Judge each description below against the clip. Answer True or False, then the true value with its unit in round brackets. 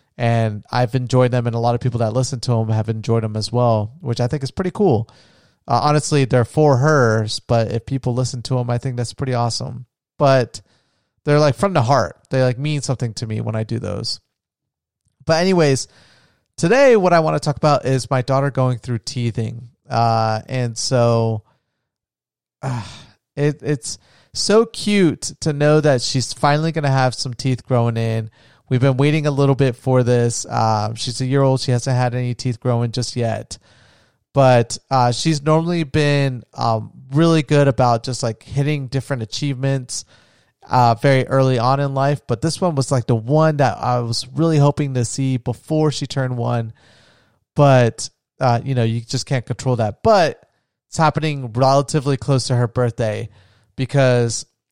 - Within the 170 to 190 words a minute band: True (185 wpm)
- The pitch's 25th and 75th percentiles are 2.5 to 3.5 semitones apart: True (3.1 semitones)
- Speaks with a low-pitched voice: True (125 Hz)